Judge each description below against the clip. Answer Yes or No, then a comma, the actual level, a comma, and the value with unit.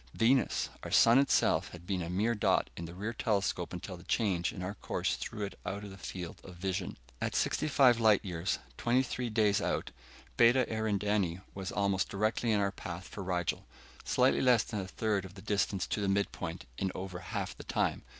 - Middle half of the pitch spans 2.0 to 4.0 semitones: Yes, average, 3.1 semitones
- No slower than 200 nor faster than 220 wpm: Yes, fast, 205 wpm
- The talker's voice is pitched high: No, low, 100 Hz